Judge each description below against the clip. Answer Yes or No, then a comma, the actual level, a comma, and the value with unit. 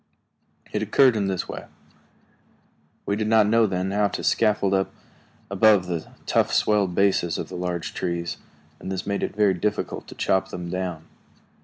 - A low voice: Yes, very low, 95 Hz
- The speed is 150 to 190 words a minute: Yes, average, 170 wpm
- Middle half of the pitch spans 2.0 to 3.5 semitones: Yes, average, 2.7 semitones